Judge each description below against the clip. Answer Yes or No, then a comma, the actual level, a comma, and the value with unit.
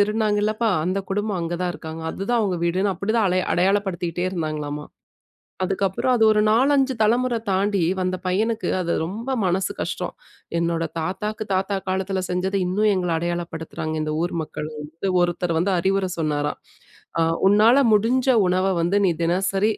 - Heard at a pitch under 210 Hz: Yes, high, 190 Hz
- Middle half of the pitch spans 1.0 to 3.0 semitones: No, average, 3.5 semitones